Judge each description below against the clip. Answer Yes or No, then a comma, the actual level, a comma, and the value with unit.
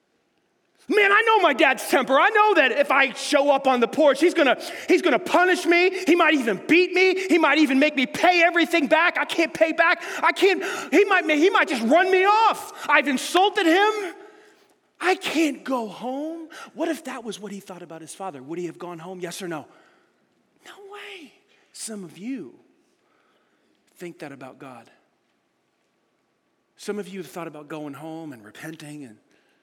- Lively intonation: Yes, wide, 9.0 semitones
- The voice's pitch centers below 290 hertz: No, very high, 315 Hz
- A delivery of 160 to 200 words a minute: Yes, average, 190 wpm